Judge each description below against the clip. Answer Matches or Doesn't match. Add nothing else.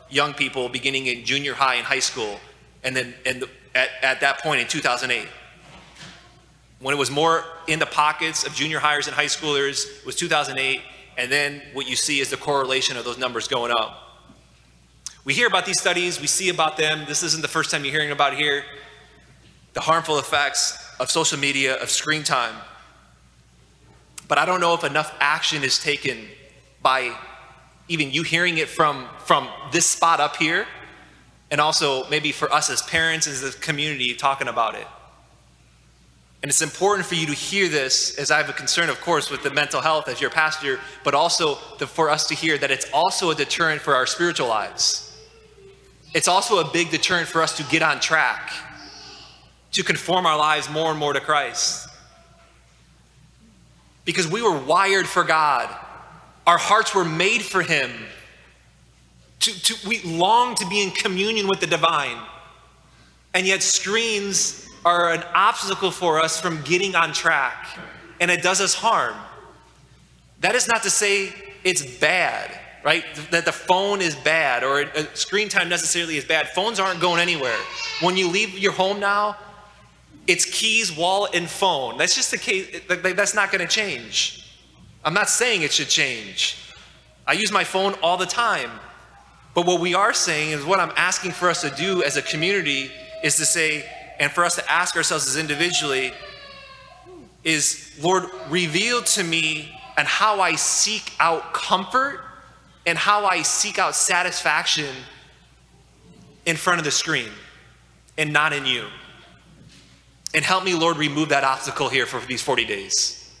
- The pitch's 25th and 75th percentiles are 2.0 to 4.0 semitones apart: Doesn't match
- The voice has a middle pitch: Matches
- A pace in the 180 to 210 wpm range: Doesn't match